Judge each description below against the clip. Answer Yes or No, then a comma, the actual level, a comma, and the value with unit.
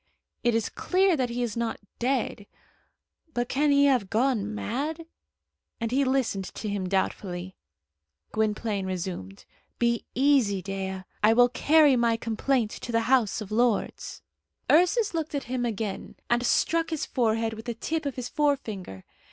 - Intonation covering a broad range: No, average, 4.5 semitones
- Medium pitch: No, high, 235 Hz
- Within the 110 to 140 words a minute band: No, average, 155 wpm